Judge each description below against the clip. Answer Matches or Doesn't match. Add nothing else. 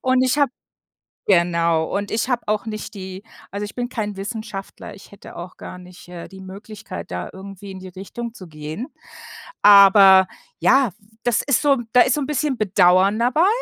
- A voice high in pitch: Matches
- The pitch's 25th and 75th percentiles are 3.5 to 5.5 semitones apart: Matches